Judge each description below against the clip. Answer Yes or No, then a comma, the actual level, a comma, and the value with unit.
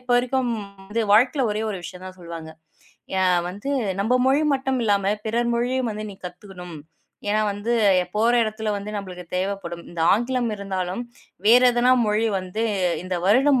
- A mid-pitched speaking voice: No, high, 210 Hz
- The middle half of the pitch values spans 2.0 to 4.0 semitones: No, average, 4.4 semitones